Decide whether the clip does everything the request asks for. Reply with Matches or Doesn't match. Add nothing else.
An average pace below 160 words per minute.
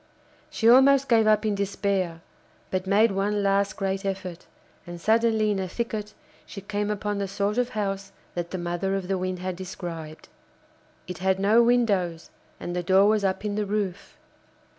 Doesn't match